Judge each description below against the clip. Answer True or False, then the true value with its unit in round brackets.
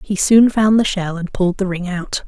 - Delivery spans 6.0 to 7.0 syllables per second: False (5.1 syllables/s)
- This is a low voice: False (190 Hz)